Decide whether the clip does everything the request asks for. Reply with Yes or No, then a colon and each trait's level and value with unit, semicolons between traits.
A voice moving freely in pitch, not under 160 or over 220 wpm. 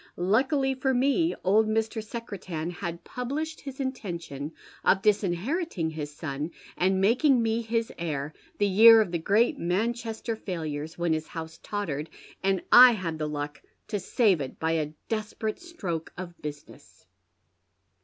No: wide, 6.3 semitones; average, 145 wpm